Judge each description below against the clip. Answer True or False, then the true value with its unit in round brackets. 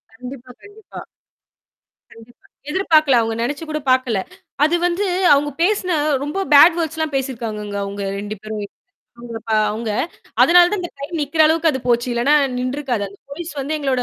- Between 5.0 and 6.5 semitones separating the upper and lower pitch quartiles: True (5.4 semitones)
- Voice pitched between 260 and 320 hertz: True (280 Hz)